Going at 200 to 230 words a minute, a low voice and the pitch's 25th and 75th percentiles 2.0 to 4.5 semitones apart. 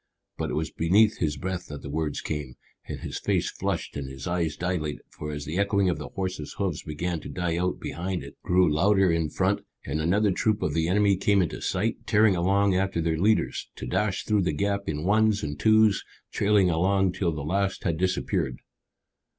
Yes: fast, 205 wpm; very low, 90 Hz; average, 4.2 semitones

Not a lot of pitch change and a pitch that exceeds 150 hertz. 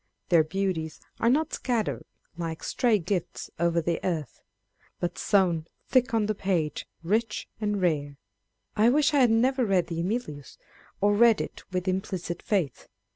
No: average, 5.0 semitones; high, 190 Hz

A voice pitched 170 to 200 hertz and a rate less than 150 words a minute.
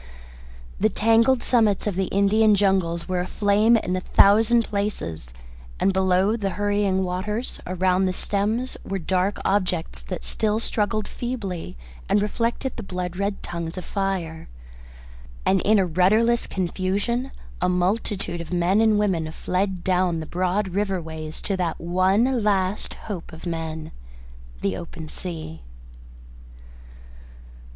Yes: high, 190 Hz; slow, 135 wpm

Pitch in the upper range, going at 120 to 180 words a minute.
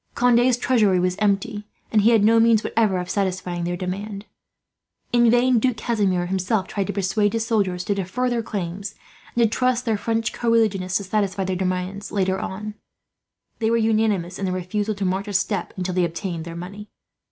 No: high, 200 Hz; average, 195 wpm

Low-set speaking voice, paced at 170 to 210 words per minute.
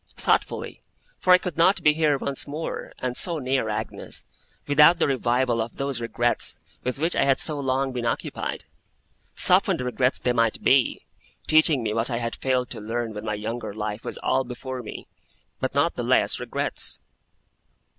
Yes: low, 125 Hz; average, 175 wpm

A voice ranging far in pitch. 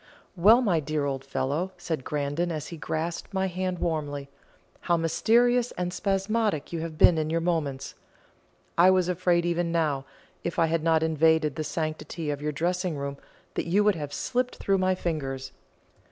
No: average, 3.2 semitones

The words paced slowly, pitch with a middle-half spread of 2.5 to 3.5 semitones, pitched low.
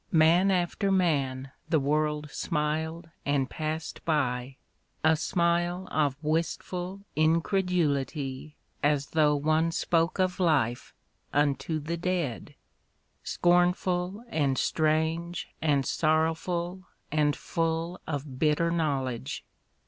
No: slow, 105 wpm; average, 2.9 semitones; medium, 160 Hz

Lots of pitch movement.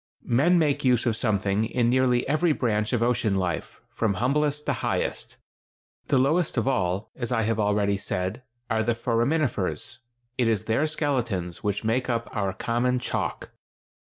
No: average, 3.8 semitones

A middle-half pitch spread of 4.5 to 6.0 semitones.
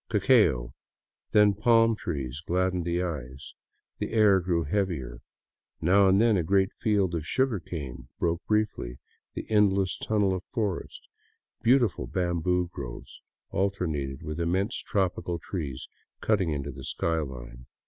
Yes: average, 5.3 semitones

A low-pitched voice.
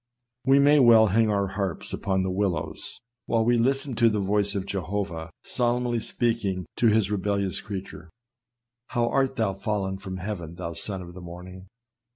Yes: low, 100 Hz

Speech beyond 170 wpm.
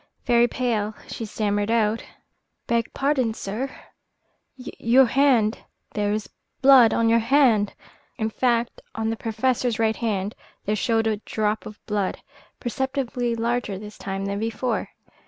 No: average, 140 wpm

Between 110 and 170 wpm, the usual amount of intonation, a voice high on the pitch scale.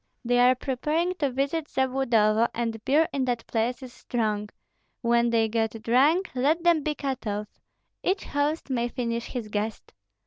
Yes: average, 165 wpm; average, 3.9 semitones; very high, 250 Hz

